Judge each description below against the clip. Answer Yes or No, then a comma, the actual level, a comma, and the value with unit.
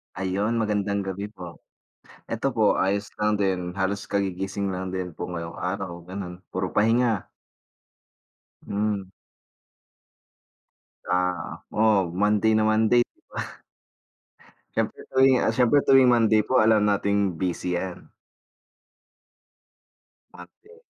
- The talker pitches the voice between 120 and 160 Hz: No, low, 100 Hz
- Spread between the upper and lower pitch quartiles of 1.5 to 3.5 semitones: Yes, average, 2.9 semitones